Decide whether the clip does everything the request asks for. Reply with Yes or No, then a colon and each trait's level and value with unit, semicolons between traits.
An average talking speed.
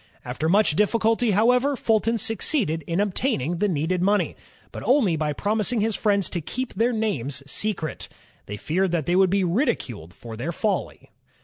Yes: average, 170 wpm